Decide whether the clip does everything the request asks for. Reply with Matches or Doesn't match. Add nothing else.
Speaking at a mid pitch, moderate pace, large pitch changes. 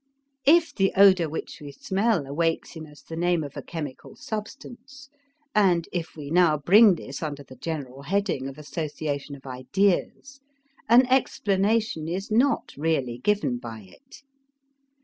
Matches